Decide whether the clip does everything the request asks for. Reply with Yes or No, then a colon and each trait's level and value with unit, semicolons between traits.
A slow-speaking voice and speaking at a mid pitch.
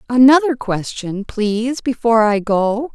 No: slow, 120 wpm; high, 230 Hz